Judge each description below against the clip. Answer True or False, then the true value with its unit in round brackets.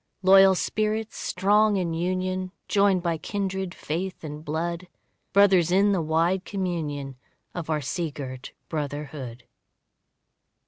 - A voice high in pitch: False (175 Hz)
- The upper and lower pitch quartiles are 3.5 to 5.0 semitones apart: True (3.8 semitones)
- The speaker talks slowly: True (120 wpm)